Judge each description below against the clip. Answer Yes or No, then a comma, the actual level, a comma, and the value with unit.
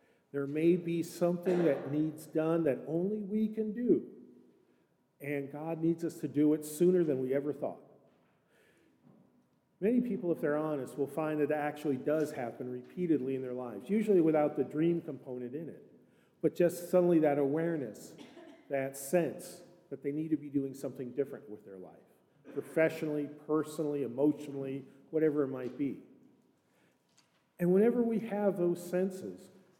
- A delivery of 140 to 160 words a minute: Yes, average, 155 wpm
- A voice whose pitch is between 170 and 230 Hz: No, medium, 155 Hz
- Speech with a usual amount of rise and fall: Yes, average, 3.9 semitones